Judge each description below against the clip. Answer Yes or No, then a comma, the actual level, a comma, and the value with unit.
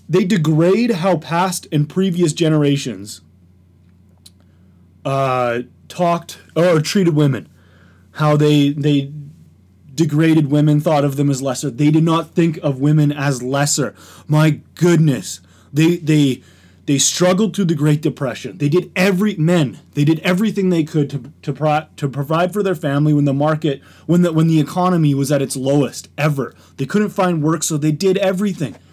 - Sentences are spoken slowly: No, average, 160 wpm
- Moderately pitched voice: Yes, medium, 150 Hz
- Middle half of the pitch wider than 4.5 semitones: No, average, 3.7 semitones